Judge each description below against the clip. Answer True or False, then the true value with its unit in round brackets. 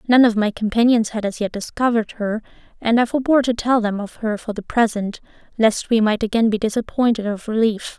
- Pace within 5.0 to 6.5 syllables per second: True (5.8 syllables/s)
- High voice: True (225 Hz)